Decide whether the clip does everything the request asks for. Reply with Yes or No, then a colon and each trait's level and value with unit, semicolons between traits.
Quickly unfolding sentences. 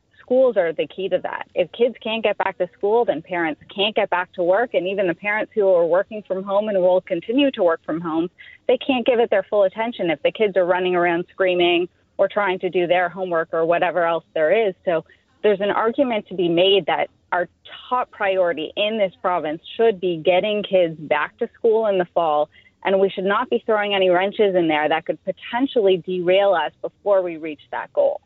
Yes: fast, 225 wpm